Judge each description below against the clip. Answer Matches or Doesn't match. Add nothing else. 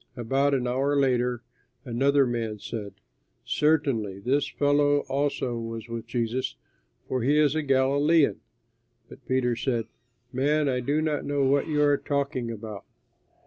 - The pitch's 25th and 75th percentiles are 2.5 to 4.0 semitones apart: Matches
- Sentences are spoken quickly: Doesn't match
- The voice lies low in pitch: Matches